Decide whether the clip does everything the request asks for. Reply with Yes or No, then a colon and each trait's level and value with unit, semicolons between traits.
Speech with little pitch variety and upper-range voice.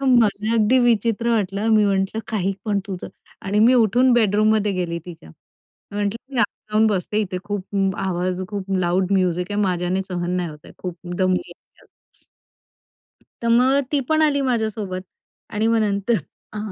No: average, 3.4 semitones; high, 205 Hz